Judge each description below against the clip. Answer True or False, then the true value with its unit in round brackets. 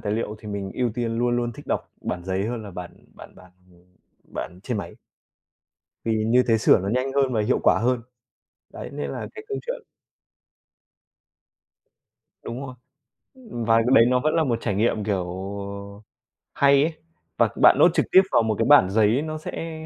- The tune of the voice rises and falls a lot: False (4.2 semitones)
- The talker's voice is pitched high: False (115 Hz)